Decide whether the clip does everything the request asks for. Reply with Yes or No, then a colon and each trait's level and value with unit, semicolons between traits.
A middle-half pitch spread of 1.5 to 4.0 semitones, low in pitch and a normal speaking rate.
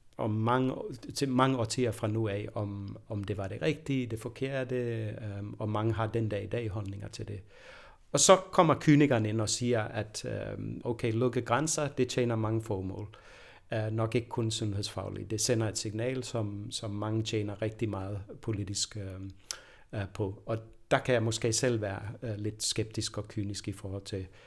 Yes: average, 2.9 semitones; low, 110 Hz; average, 185 wpm